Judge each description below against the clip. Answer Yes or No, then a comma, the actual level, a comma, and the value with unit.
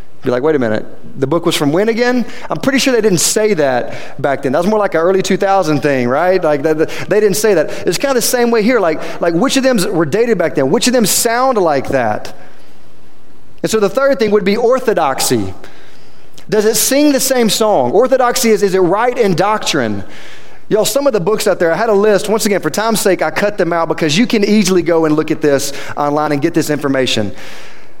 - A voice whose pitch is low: No, high, 200 Hz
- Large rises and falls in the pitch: Yes, wide, 6.4 semitones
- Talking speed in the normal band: No, fast, 240 wpm